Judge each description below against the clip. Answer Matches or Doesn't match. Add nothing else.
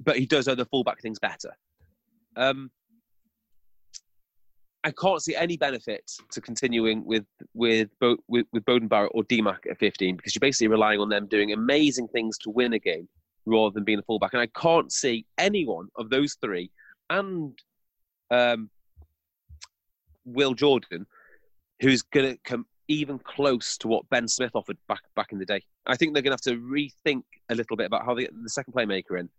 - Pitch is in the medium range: Doesn't match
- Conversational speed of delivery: Matches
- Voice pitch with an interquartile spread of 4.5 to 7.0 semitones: Matches